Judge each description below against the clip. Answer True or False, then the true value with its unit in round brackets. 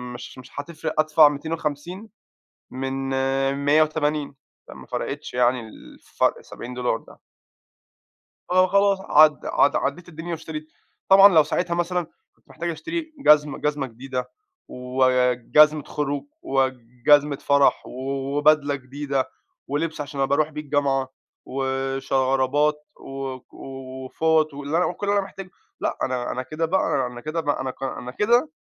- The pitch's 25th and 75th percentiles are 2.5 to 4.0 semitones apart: True (3.1 semitones)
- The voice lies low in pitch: False (145 Hz)